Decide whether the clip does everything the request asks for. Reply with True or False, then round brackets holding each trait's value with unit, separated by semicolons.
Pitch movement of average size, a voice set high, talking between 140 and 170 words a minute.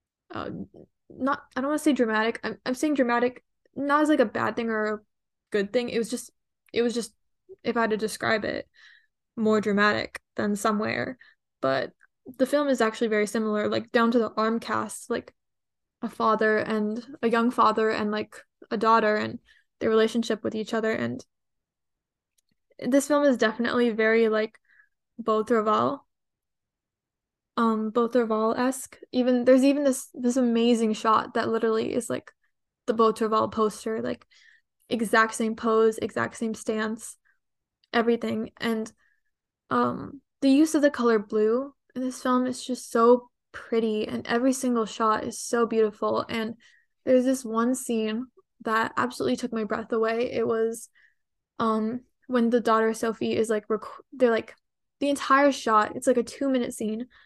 False (2.3 semitones; 230 Hz; 160 wpm)